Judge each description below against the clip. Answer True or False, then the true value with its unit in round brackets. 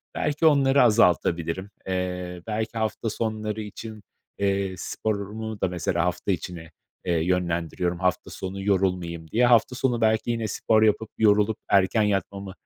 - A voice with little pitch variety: False (3.4 semitones)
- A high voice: False (100 Hz)